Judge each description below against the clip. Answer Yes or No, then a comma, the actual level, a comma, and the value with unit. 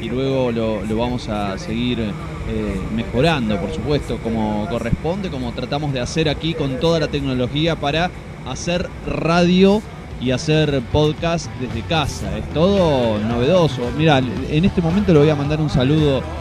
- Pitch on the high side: No, low, 135 Hz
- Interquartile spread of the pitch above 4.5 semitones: Yes, average, 5.3 semitones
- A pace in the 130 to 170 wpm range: Yes, average, 155 wpm